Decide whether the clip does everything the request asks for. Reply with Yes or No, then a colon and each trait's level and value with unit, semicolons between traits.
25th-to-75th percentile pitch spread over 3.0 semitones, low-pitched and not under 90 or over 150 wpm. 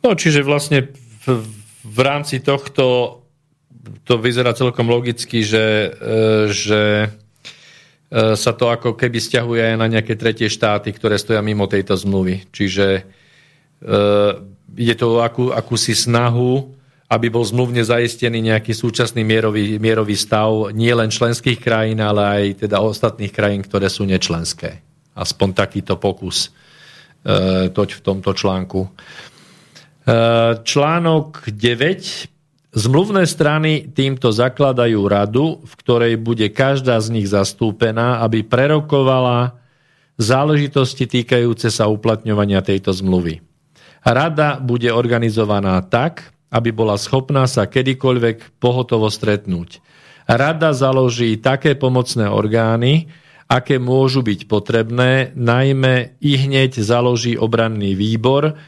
Yes: average, 3.7 semitones; low, 115 Hz; slow, 110 wpm